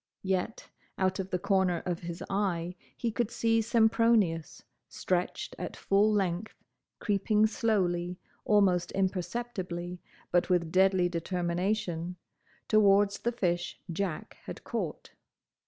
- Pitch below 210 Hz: Yes, high, 190 Hz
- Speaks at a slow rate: Yes, slow, 115 wpm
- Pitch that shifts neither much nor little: Yes, average, 3.2 semitones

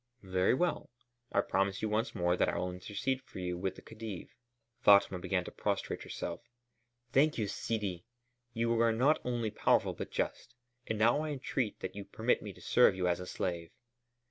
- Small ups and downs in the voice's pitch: No, average, 4.3 semitones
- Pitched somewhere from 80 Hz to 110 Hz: Yes, low, 105 Hz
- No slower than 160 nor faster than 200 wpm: Yes, average, 190 wpm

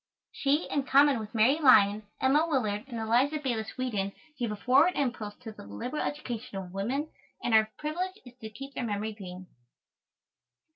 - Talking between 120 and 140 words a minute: No, average, 175 wpm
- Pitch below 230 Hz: No, high, 240 Hz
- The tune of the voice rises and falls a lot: No, average, 4.8 semitones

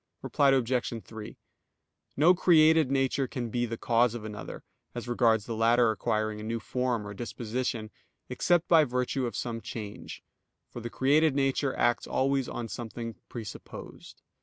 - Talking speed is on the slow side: No, average, 155 wpm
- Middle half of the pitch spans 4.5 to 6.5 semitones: No, average, 2.9 semitones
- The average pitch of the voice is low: Yes, low, 120 Hz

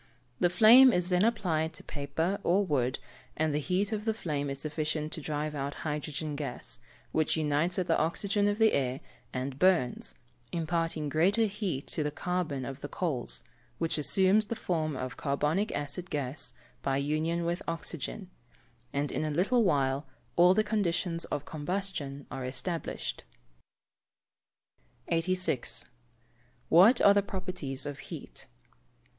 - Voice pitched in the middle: Yes, medium, 160 Hz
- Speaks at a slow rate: No, average, 150 wpm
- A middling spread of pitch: Yes, average, 4.4 semitones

